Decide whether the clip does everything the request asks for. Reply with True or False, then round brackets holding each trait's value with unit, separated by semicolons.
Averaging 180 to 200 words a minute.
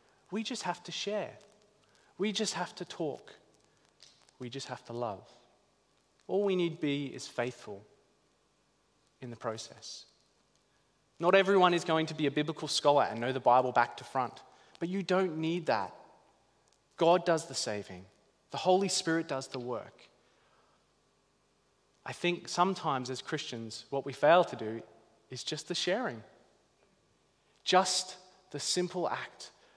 False (145 wpm)